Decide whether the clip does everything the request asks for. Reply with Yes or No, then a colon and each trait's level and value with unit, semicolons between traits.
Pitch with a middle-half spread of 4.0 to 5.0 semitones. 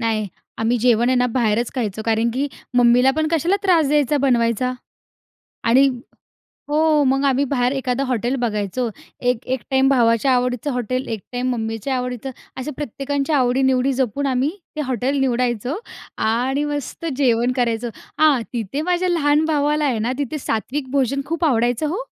No: average, 3.1 semitones